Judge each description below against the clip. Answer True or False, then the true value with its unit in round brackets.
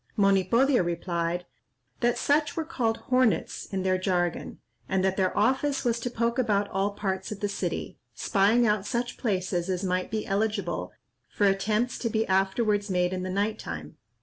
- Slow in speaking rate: False (175 wpm)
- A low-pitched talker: False (200 Hz)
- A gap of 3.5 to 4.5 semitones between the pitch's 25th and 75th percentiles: True (3.8 semitones)